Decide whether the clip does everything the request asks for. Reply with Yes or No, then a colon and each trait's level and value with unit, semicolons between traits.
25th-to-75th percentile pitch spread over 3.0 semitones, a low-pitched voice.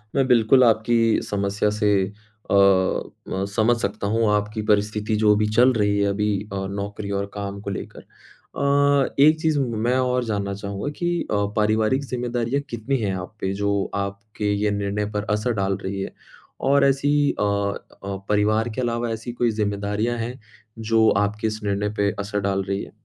No: average, 2.7 semitones; low, 105 Hz